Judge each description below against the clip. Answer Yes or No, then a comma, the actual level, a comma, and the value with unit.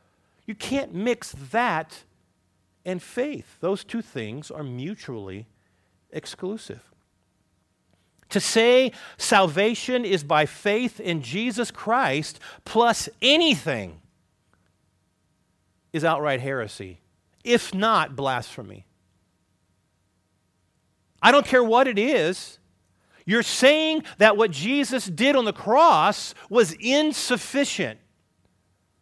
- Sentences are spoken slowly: Yes, slow, 95 wpm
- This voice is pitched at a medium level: Yes, medium, 165 Hz